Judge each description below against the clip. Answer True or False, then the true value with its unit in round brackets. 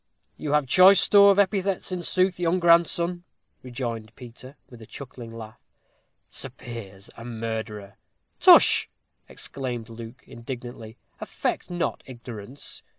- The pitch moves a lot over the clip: True (7.1 semitones)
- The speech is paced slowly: True (125 wpm)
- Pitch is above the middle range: False (125 Hz)